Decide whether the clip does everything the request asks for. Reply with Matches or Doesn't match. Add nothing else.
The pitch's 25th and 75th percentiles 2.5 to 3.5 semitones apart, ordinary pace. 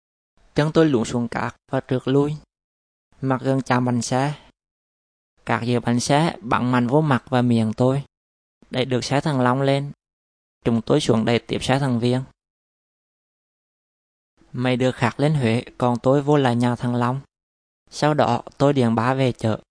Matches